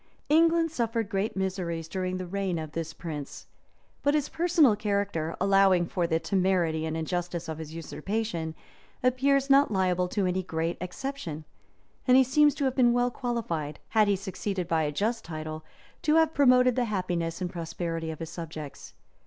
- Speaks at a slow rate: No, average, 170 wpm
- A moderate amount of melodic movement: No, wide, 6.7 semitones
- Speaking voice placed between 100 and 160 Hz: No, medium, 185 Hz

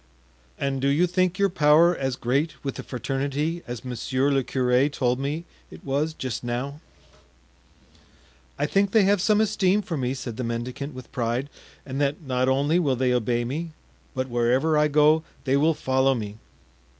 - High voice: No, medium, 140 Hz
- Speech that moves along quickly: No, average, 175 wpm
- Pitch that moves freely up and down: No, average, 3.8 semitones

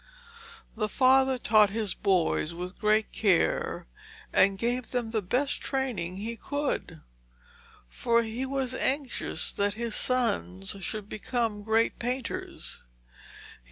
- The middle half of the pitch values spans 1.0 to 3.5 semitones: No, average, 4.0 semitones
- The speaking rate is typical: No, slow, 120 wpm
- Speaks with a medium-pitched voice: No, high, 225 Hz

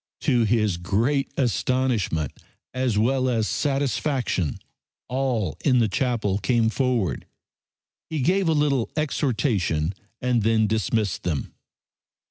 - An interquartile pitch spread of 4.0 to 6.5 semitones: Yes, average, 4.4 semitones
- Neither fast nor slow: No, slow, 110 wpm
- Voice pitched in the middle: No, low, 120 Hz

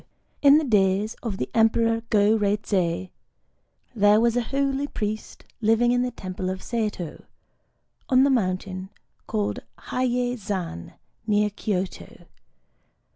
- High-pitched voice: Yes, high, 215 Hz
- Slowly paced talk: Yes, slow, 125 wpm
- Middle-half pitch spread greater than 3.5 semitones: Yes, average, 4.0 semitones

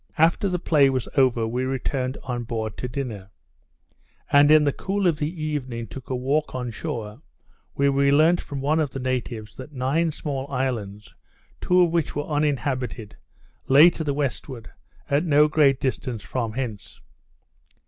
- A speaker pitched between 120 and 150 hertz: Yes, low, 135 Hz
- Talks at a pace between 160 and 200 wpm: Yes, average, 170 wpm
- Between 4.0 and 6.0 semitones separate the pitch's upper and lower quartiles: No, average, 3.3 semitones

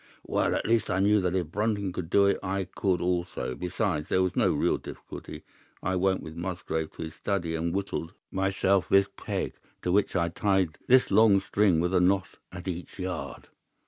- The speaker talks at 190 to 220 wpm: Yes, average, 195 wpm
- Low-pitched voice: Yes, very low, 95 Hz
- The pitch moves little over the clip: Yes, narrow, 2.1 semitones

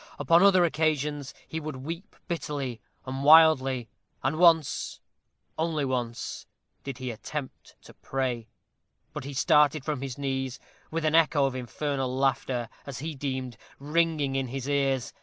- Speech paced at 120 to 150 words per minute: Yes, average, 145 wpm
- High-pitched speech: No, medium, 140 Hz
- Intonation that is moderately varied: Yes, average, 3.0 semitones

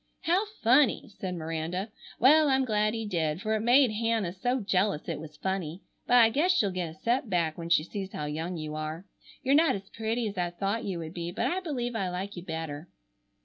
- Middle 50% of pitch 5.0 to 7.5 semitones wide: Yes, wide, 5.5 semitones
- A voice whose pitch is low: No, high, 195 Hz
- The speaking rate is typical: No, fast, 225 wpm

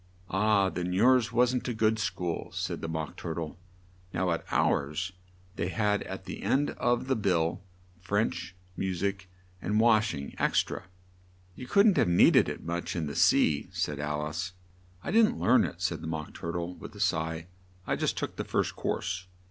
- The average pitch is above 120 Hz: No, very low, 90 Hz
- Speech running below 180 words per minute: No, average, 190 wpm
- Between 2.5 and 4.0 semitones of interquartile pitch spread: No, average, 4.4 semitones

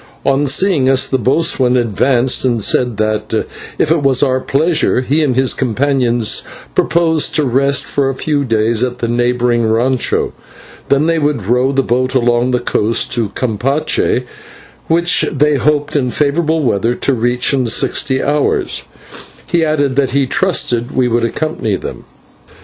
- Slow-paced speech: No, average, 155 wpm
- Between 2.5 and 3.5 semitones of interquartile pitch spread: Yes, average, 3.1 semitones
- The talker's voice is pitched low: Yes, low, 130 Hz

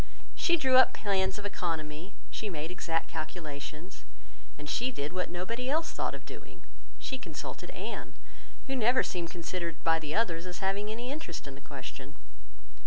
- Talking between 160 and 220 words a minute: Yes, average, 170 wpm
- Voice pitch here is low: No, medium, 180 Hz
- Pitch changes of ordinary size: No, wide, 6.5 semitones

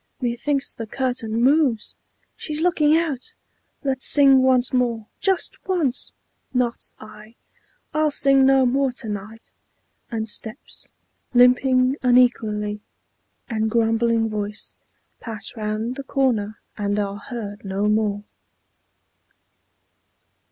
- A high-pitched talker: Yes, high, 240 Hz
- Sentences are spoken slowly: Yes, slow, 110 wpm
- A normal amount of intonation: Yes, average, 3.7 semitones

